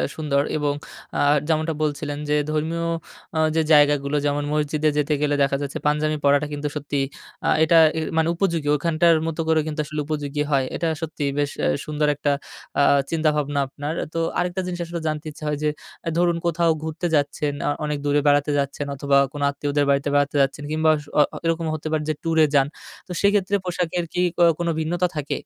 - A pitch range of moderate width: No, narrow, 2.1 semitones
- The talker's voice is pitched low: No, medium, 150 Hz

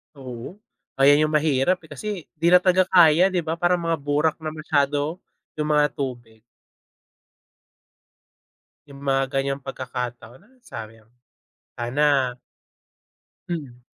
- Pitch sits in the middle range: Yes, medium, 145 Hz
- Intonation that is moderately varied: Yes, average, 3.6 semitones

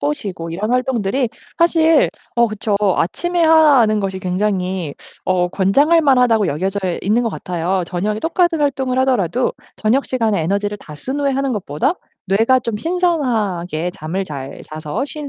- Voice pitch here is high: Yes, high, 215 Hz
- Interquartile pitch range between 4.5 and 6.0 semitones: No, wide, 6.5 semitones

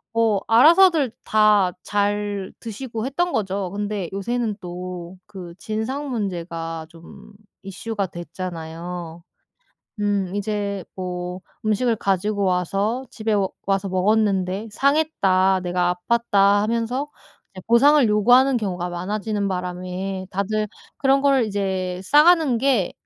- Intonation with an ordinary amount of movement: Yes, average, 3.7 semitones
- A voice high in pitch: Yes, high, 200 Hz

